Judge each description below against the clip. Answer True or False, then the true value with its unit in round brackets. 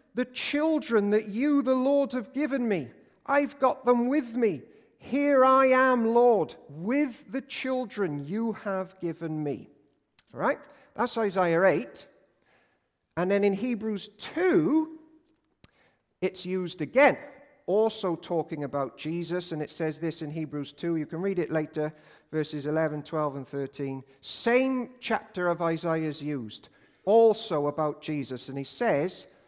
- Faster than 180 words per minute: False (145 wpm)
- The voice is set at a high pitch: True (195 Hz)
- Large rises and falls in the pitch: True (8.7 semitones)